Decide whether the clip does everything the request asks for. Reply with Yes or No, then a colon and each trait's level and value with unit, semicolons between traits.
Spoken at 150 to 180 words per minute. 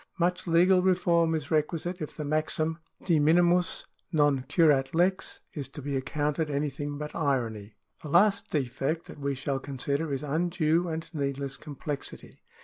Yes: average, 155 wpm